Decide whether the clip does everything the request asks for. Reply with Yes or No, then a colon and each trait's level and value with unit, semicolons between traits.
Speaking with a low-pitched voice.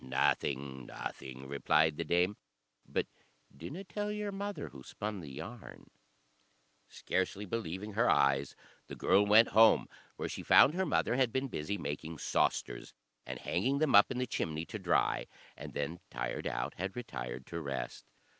Yes: very low, 95 Hz